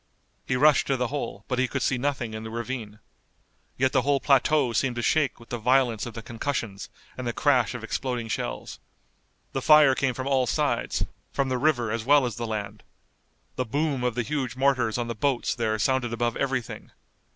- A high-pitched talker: No, low, 125 Hz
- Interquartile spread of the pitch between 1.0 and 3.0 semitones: Yes, average, 2.7 semitones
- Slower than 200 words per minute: No, fast, 205 wpm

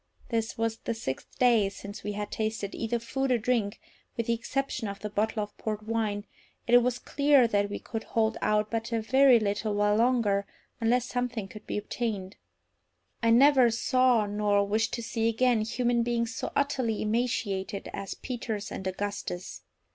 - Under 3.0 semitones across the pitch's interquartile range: Yes, narrow, 2.6 semitones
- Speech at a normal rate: Yes, average, 180 wpm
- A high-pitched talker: Yes, high, 225 Hz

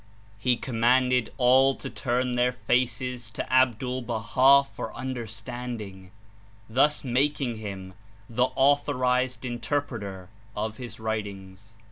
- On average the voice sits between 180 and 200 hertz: No, low, 125 Hz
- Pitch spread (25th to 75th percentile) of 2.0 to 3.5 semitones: Yes, narrow, 2.6 semitones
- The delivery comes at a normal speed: No, slow, 105 wpm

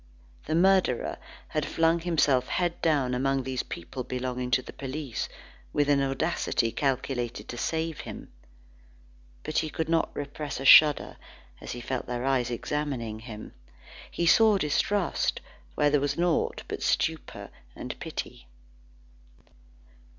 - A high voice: No, medium, 140 Hz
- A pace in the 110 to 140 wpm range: Yes, slow, 135 wpm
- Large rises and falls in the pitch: No, average, 4.2 semitones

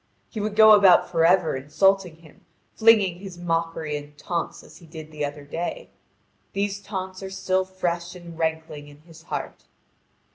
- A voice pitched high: No, medium, 175 Hz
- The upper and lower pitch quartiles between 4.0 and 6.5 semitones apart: No, average, 3.2 semitones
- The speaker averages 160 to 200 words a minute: Yes, average, 170 wpm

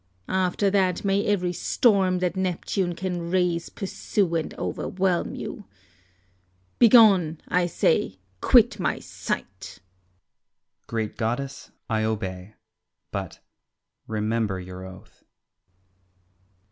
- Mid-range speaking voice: Yes, medium, 175 Hz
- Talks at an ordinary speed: No, slow, 100 wpm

